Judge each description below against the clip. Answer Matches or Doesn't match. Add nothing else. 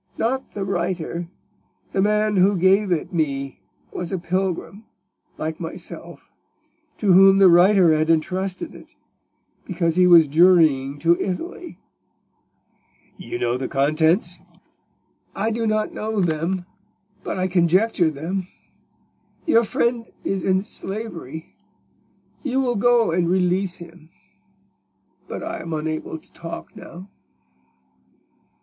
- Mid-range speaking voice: Matches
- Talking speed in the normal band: Doesn't match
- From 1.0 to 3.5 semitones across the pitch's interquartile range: Matches